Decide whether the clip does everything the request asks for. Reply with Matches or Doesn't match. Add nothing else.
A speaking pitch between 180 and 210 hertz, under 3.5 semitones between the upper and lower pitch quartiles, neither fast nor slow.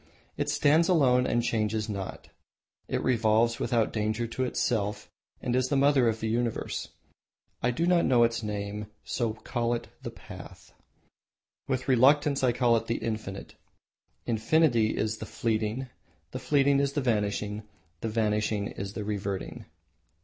Doesn't match